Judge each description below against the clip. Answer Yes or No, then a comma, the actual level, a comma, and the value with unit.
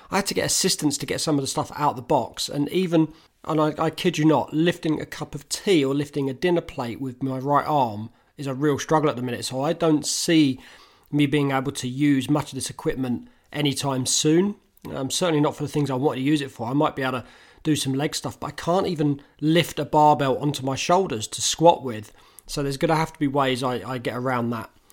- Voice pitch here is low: No, medium, 145 Hz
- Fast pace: Yes, fast, 255 wpm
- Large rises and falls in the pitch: No, average, 2.8 semitones